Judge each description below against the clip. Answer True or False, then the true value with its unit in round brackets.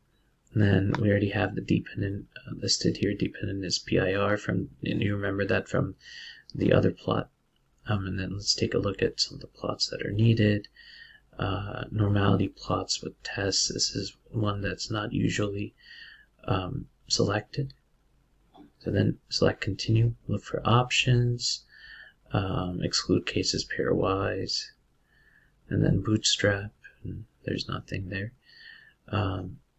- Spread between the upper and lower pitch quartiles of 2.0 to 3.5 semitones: True (2.7 semitones)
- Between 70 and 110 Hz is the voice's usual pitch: True (105 Hz)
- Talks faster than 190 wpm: False (140 wpm)